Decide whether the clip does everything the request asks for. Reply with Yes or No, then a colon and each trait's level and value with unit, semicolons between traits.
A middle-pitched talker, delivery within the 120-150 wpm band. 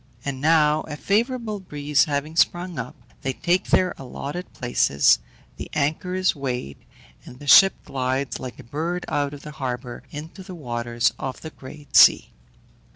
No: medium, 145 Hz; average, 160 wpm